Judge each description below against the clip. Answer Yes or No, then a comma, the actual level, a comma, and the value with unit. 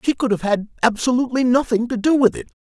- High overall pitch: Yes, high, 240 Hz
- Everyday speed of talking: No, fast, 230 wpm